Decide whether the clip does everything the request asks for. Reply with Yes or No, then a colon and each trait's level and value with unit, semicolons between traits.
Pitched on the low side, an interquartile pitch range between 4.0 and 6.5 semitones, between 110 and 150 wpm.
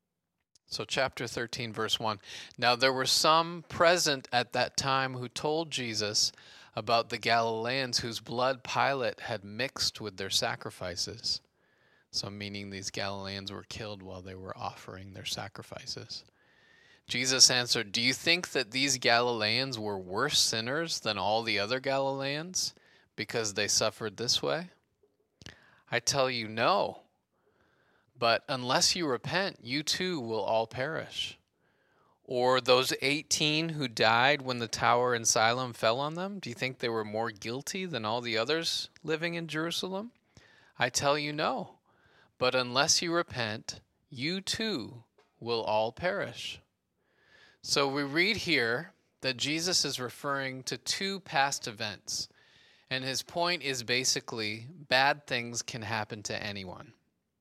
Yes: low, 125 Hz; average, 4.5 semitones; average, 140 wpm